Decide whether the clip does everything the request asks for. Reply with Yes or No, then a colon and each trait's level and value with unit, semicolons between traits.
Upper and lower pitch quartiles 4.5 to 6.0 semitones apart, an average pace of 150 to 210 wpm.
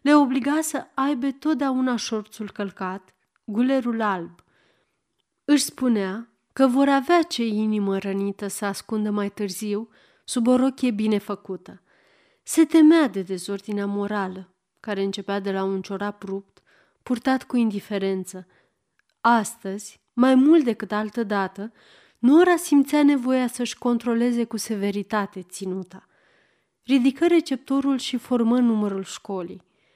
No: average, 4.9 semitones; average, 120 wpm